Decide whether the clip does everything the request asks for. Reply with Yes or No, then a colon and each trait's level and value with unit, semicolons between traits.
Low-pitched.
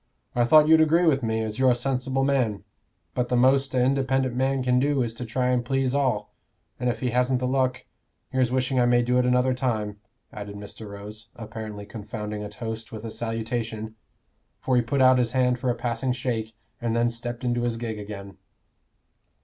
Yes: low, 120 Hz